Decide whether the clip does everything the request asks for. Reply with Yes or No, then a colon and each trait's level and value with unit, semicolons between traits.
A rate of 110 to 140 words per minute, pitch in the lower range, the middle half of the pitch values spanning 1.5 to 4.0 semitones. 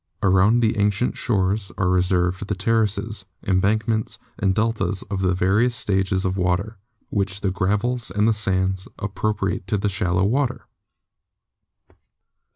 Yes: slow, 135 wpm; low, 100 Hz; narrow, 2.5 semitones